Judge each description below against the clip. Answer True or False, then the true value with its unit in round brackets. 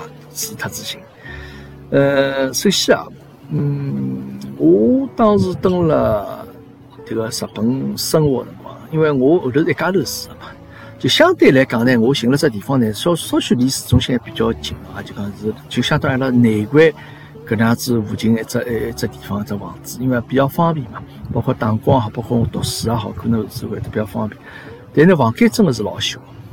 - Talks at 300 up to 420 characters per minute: False (275 characters per minute)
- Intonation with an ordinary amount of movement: True (4.8 semitones)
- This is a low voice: True (125 Hz)